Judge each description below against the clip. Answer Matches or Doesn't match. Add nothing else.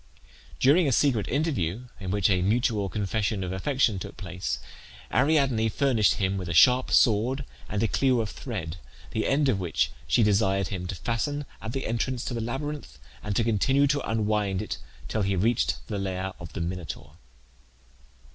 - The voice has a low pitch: Matches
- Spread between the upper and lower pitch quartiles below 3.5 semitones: Doesn't match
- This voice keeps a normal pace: Matches